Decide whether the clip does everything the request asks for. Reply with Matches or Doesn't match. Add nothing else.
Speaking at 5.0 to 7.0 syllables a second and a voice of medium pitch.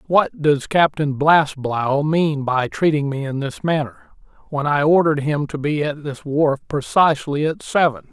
Doesn't match